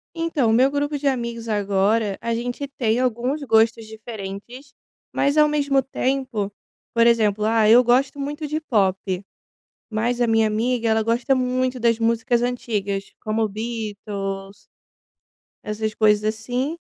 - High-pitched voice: Yes, high, 230 Hz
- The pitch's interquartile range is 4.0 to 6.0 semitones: No, average, 3.0 semitones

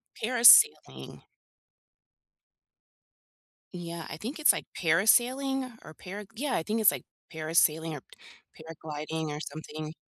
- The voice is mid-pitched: Yes, medium, 170 Hz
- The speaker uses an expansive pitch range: Yes, wide, 7.3 semitones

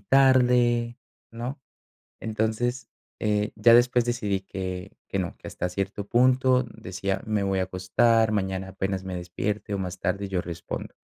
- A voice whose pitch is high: No, low, 105 Hz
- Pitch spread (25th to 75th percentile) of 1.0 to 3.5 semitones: No, average, 4.0 semitones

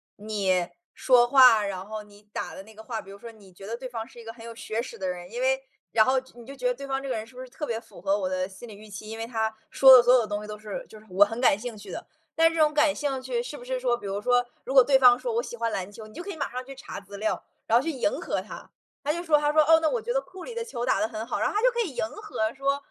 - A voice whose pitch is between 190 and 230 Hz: No, high, 240 Hz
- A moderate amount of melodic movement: Yes, average, 4.4 semitones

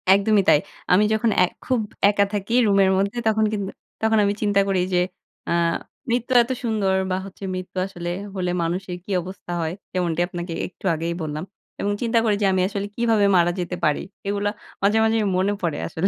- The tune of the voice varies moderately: Yes, average, 3.0 semitones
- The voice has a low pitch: No, high, 195 Hz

